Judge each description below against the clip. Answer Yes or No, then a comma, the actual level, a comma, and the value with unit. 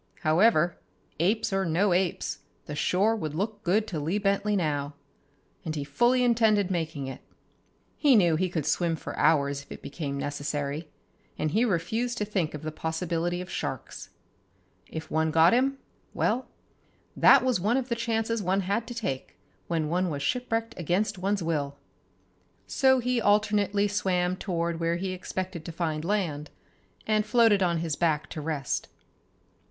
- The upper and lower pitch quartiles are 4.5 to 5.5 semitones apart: Yes, average, 5.1 semitones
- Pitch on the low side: No, medium, 180 Hz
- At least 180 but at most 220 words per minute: No, average, 165 wpm